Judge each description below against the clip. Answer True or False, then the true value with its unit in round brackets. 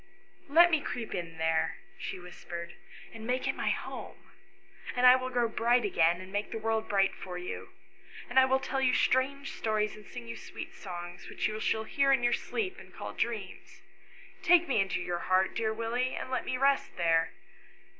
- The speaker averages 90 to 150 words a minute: False (205 wpm)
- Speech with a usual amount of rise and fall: False (6.3 semitones)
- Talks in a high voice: True (220 Hz)